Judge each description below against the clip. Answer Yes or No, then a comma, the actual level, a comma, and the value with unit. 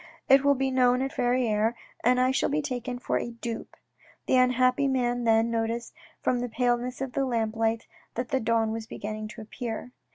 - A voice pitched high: Yes, high, 245 Hz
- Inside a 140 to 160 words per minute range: No, average, 190 wpm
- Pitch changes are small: Yes, narrow, 2.0 semitones